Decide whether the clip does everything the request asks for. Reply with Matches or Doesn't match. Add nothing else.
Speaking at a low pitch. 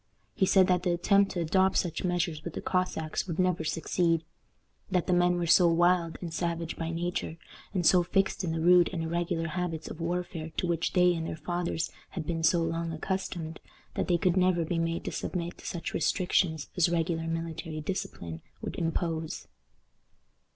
Doesn't match